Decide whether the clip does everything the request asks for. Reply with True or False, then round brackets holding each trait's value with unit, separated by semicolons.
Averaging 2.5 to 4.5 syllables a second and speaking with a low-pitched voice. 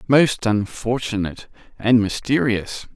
True (4.1 syllables/s; 115 Hz)